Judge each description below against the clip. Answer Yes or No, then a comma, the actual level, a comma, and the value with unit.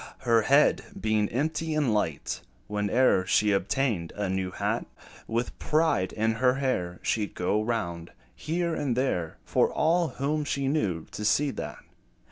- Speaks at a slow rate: No, average, 155 wpm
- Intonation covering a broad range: Yes, wide, 6.1 semitones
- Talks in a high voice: No, low, 115 Hz